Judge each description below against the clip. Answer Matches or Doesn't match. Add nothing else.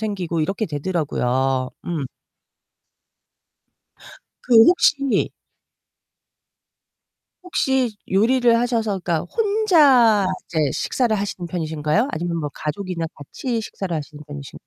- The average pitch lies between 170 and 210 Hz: Matches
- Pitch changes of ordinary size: Doesn't match